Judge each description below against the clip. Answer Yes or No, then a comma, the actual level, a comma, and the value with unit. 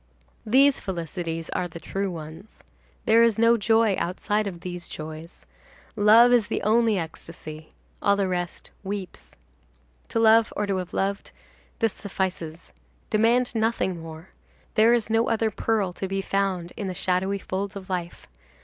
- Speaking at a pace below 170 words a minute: Yes, average, 150 wpm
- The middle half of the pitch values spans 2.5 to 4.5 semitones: Yes, average, 4.0 semitones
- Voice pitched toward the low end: No, high, 195 Hz